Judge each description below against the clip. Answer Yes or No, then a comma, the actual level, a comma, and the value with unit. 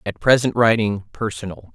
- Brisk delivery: No, slow, 105 wpm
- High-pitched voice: No, low, 110 Hz